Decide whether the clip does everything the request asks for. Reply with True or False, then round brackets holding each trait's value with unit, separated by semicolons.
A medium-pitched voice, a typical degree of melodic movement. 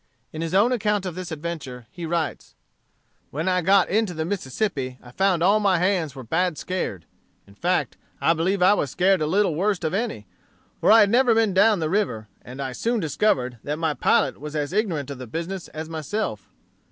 True (170 Hz; 5.0 semitones)